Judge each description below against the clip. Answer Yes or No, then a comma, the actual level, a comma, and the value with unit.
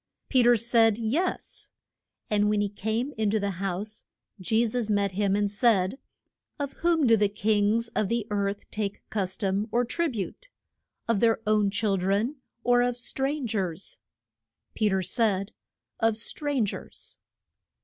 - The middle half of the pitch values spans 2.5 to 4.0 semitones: Yes, average, 2.9 semitones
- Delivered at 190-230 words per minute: No, average, 160 wpm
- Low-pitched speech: No, high, 215 Hz